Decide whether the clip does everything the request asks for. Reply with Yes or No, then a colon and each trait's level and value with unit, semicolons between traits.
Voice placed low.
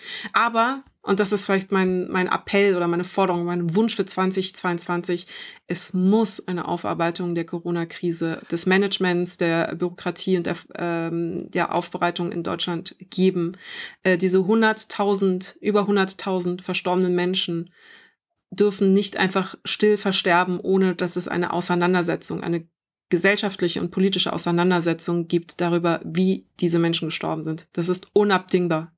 No: medium, 180 Hz